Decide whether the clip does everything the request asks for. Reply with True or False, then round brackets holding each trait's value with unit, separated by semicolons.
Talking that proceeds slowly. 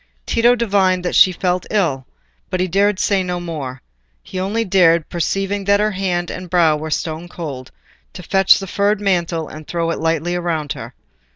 False (185 wpm)